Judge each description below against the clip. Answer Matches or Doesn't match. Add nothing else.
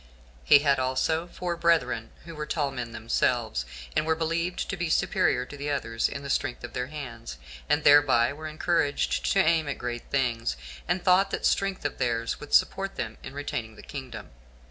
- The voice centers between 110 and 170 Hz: Matches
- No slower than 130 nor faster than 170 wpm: Doesn't match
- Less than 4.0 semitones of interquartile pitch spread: Doesn't match